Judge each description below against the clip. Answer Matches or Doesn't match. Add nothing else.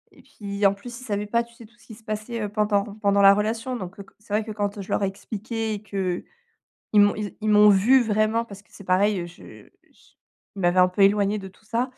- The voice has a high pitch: Matches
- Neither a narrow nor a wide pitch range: Doesn't match